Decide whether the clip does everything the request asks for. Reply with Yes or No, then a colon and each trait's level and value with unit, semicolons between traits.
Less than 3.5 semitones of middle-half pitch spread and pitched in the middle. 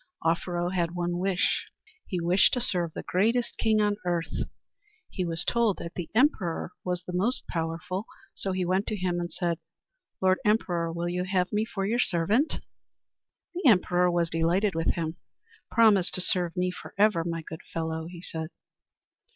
Yes: average, 2.8 semitones; medium, 180 Hz